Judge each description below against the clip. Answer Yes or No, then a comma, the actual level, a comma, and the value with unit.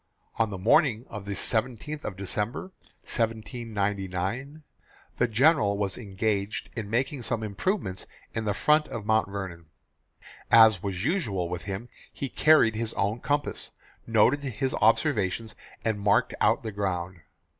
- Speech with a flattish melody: No, average, 3.8 semitones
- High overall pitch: No, low, 110 Hz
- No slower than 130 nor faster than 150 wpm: Yes, average, 140 wpm